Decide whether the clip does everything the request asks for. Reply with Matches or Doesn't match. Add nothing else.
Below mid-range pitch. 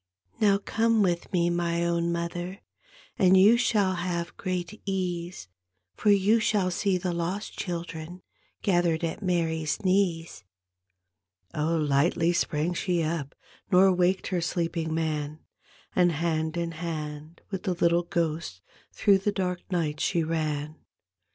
Doesn't match